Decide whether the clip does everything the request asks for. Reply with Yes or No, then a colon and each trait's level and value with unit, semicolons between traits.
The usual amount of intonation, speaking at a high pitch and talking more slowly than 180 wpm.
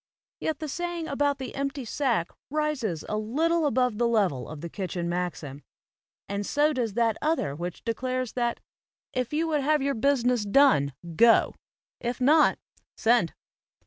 No: wide, 5.9 semitones; high, 245 Hz; average, 155 wpm